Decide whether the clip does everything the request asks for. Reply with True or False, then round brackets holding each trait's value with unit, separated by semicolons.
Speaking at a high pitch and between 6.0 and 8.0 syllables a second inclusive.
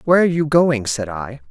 False (135 Hz; 6.1 syllables/s)